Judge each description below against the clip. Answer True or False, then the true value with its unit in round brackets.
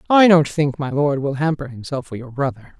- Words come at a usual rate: False (235 wpm)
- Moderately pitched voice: True (145 Hz)